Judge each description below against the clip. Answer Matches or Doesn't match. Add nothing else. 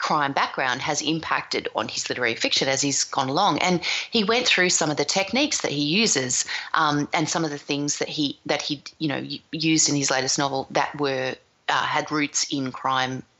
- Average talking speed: Doesn't match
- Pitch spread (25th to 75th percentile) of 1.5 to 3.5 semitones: Matches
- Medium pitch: Matches